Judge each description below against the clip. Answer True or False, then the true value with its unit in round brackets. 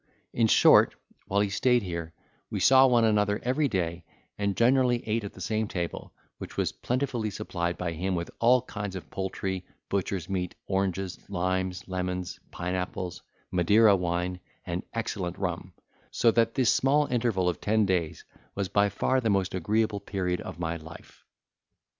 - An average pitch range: True (3.8 semitones)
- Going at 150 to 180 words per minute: True (165 wpm)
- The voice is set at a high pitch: False (95 Hz)